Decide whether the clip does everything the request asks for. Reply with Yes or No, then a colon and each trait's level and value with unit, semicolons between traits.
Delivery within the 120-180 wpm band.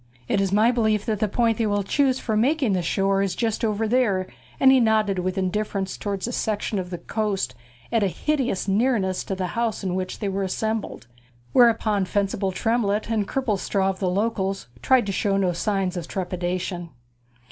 No: average, 190 wpm